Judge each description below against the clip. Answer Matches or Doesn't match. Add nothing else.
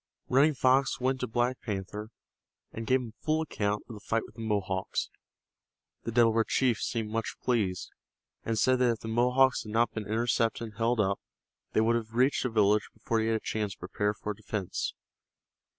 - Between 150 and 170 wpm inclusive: Doesn't match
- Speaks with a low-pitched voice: Matches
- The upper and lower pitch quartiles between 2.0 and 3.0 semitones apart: Matches